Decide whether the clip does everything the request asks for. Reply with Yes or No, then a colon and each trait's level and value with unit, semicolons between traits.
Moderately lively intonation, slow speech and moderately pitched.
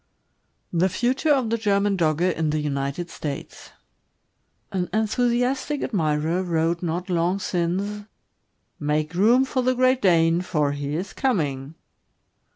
No: wide, 5.8 semitones; slow, 130 wpm; medium, 180 Hz